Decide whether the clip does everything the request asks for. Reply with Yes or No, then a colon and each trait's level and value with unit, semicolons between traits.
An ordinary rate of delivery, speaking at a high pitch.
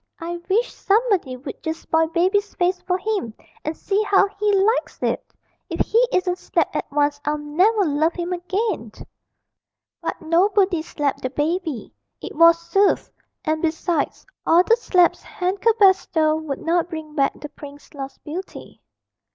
Yes: average, 160 wpm; very high, 345 Hz